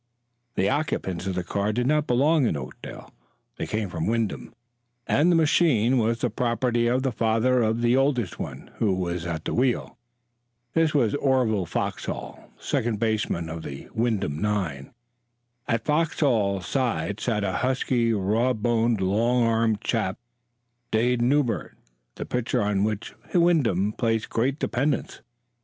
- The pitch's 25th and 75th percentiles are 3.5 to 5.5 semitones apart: Yes, average, 3.8 semitones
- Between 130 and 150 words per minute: Yes, average, 145 wpm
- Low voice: Yes, low, 115 Hz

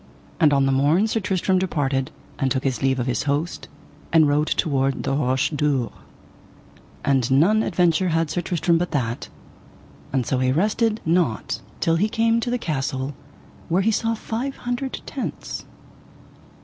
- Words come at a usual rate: Yes, average, 160 wpm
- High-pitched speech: No, medium, 155 Hz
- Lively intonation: Yes, wide, 6.0 semitones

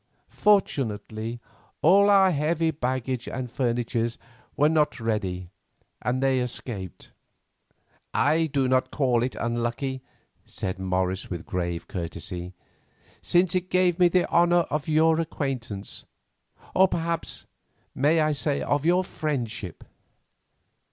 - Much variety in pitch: Yes, wide, 6.3 semitones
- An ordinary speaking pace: No, slow, 115 wpm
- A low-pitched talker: Yes, low, 130 Hz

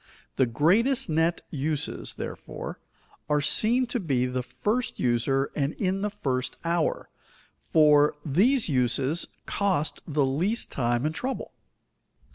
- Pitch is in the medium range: Yes, medium, 155 Hz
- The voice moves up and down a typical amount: No, wide, 7.0 semitones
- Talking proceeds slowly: Yes, slow, 130 wpm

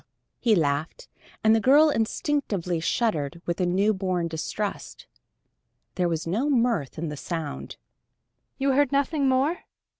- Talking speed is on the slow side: Yes, slow, 130 wpm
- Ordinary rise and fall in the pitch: No, wide, 7.9 semitones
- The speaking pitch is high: Yes, high, 205 Hz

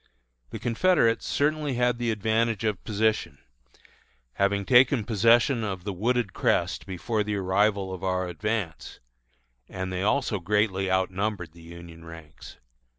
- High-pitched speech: No, low, 105 Hz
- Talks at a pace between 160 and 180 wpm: No, slow, 135 wpm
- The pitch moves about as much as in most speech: Yes, average, 3.7 semitones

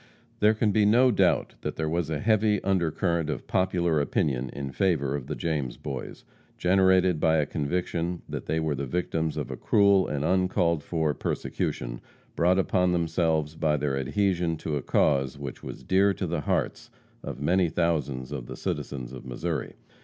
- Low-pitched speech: Yes, very low, 80 Hz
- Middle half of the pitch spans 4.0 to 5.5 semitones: Yes, average, 4.3 semitones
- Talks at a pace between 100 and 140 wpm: No, average, 175 wpm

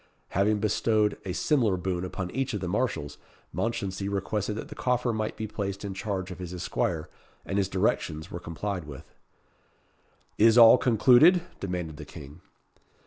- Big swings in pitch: No, average, 3.4 semitones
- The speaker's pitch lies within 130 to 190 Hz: No, low, 100 Hz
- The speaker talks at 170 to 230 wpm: No, average, 160 wpm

